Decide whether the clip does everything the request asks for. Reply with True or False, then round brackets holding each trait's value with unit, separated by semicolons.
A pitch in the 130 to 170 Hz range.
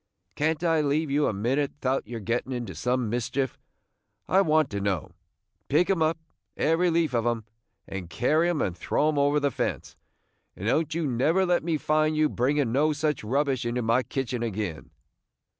True (140 Hz)